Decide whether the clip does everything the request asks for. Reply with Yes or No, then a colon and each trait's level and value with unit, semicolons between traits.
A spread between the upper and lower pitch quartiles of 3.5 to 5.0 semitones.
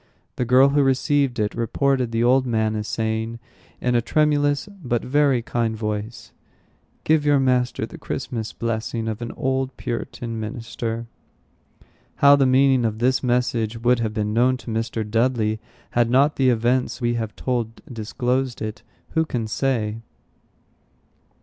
No: average, 2.7 semitones